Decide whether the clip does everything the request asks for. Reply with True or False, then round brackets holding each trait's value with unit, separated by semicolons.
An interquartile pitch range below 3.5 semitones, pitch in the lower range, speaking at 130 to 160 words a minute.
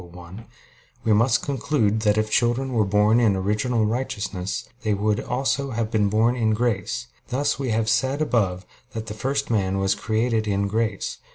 False (2.9 semitones; 110 Hz; 180 wpm)